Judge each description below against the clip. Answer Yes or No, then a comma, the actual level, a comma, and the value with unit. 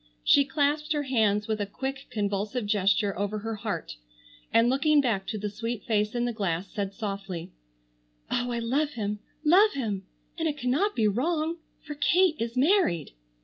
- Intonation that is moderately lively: No, wide, 6.0 semitones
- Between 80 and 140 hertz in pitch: No, high, 230 Hz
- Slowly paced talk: No, average, 175 wpm